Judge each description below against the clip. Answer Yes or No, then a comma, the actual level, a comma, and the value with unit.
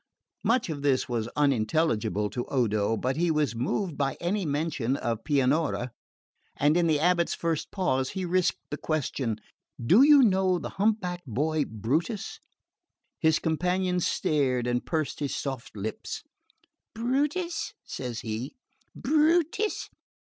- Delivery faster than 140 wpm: No, slow, 135 wpm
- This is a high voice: No, medium, 155 Hz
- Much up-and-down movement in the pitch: Yes, wide, 6.4 semitones